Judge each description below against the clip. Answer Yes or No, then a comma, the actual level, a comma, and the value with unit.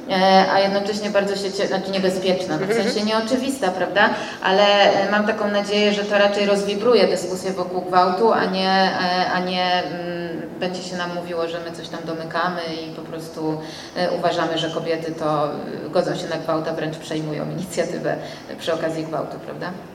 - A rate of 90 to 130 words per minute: No, average, 155 wpm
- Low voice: No, medium, 180 Hz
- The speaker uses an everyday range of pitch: Yes, average, 3.2 semitones